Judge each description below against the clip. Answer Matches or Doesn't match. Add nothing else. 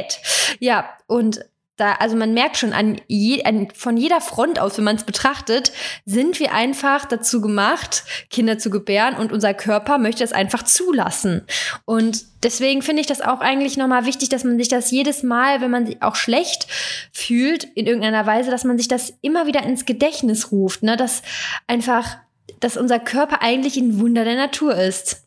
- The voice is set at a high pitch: Matches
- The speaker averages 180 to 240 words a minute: Matches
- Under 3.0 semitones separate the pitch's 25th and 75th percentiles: Doesn't match